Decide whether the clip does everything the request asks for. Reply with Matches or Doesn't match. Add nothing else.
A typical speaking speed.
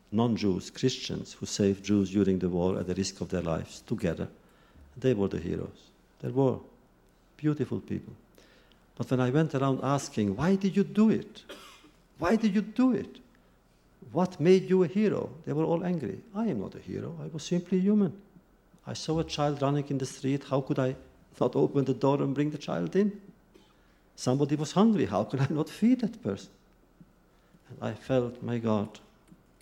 Matches